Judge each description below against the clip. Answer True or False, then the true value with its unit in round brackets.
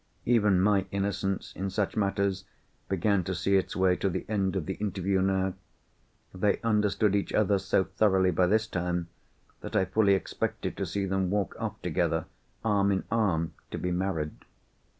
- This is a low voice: True (95 Hz)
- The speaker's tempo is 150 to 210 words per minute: True (170 wpm)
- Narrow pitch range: True (1.4 semitones)